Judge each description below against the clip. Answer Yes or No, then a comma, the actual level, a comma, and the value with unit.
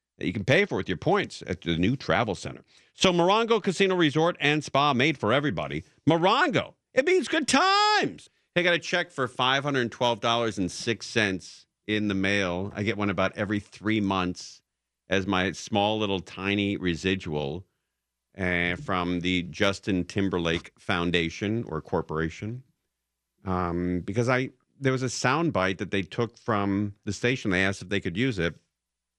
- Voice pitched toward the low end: Yes, low, 100 Hz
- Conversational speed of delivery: Yes, average, 160 wpm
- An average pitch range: No, wide, 6.1 semitones